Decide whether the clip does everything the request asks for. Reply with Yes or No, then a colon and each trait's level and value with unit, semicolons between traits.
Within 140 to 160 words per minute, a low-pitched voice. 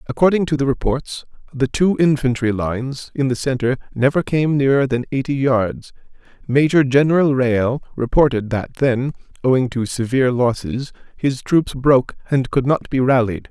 Yes: average, 155 wpm; low, 130 Hz